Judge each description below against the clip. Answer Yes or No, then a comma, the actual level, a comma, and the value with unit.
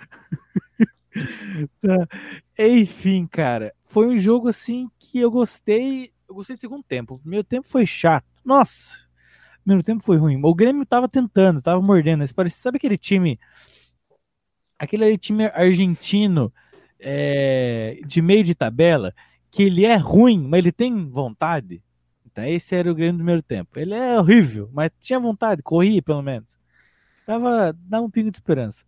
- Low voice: No, medium, 185 Hz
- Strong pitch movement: Yes, wide, 6.5 semitones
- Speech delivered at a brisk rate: No, average, 155 wpm